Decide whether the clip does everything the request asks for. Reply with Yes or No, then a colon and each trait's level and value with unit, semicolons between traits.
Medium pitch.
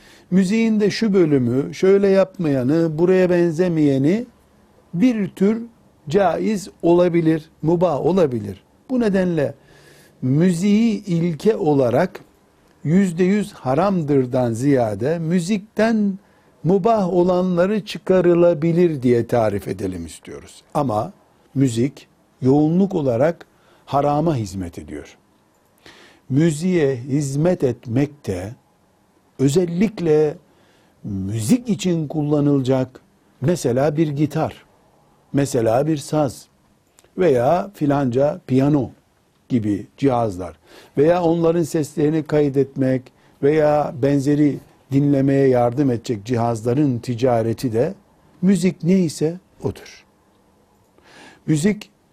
Yes: medium, 155 Hz